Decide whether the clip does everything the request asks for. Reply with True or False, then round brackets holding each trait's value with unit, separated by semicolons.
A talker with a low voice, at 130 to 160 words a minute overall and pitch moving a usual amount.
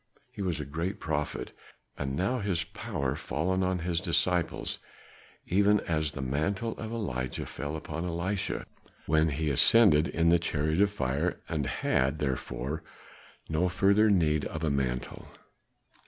True (80 Hz; 150 wpm; 4.1 semitones)